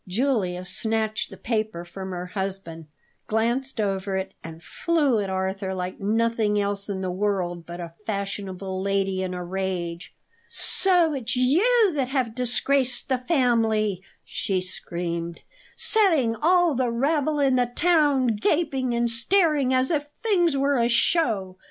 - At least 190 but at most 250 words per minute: No, average, 150 wpm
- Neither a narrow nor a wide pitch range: No, wide, 6.2 semitones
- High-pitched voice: Yes, high, 225 Hz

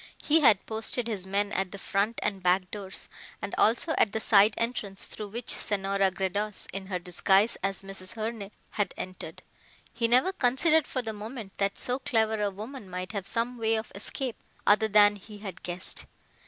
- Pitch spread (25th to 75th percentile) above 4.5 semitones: No, average, 2.8 semitones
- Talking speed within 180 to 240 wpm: Yes, average, 185 wpm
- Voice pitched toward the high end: Yes, high, 205 Hz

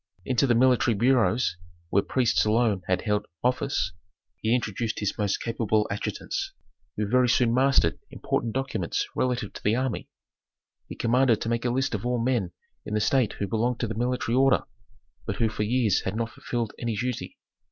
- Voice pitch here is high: No, low, 115 Hz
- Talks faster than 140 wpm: Yes, average, 180 wpm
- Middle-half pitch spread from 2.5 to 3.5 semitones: Yes, average, 2.8 semitones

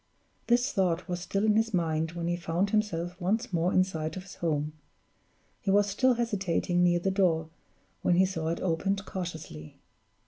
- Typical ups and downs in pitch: Yes, average, 3.1 semitones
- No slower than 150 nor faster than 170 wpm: No, average, 180 wpm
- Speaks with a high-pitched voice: No, medium, 180 Hz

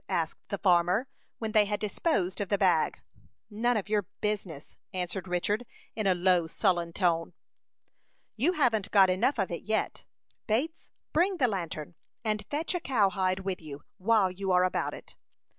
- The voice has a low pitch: No, high, 195 Hz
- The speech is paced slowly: No, average, 165 wpm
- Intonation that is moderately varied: Yes, average, 3.4 semitones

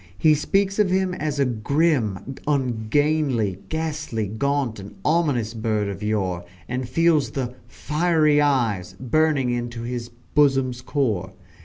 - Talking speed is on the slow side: Yes, slow, 130 wpm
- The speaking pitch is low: Yes, low, 130 Hz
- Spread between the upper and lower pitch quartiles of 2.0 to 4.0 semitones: No, wide, 5.4 semitones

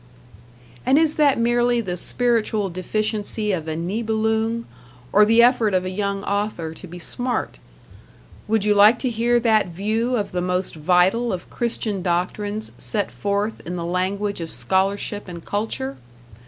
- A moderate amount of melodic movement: Yes, average, 3.8 semitones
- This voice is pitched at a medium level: No, high, 205 Hz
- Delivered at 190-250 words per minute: No, average, 155 wpm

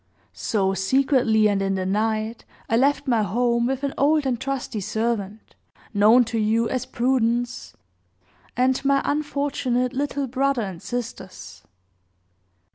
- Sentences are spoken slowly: Yes, slow, 130 wpm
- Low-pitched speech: No, high, 240 Hz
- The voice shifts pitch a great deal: No, average, 3.6 semitones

